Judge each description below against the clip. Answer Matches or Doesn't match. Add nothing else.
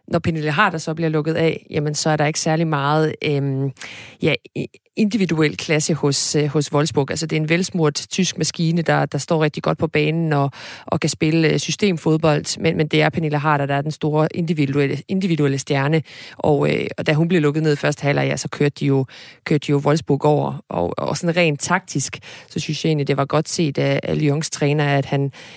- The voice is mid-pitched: Matches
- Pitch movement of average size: Doesn't match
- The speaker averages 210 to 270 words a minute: Matches